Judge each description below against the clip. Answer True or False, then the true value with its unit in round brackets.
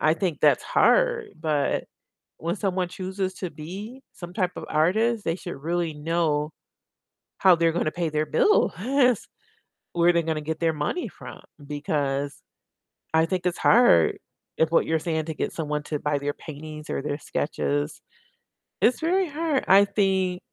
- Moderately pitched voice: True (165 Hz)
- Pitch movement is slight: False (3.8 semitones)